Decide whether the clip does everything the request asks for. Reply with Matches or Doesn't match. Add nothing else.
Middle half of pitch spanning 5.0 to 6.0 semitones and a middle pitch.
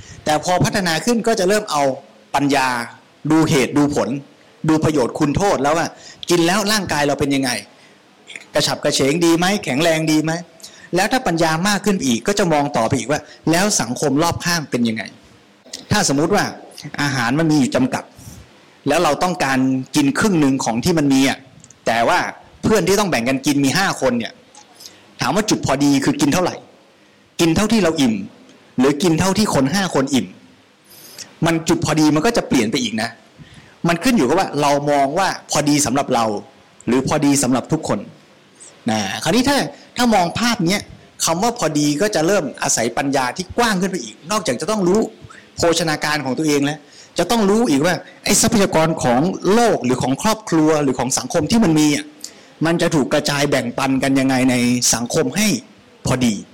Matches